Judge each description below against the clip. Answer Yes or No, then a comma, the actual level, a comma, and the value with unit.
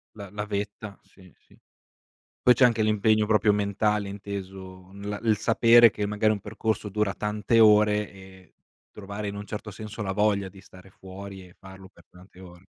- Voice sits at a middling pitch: No, low, 105 Hz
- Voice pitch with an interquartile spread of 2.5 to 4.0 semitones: No, narrow, 1.8 semitones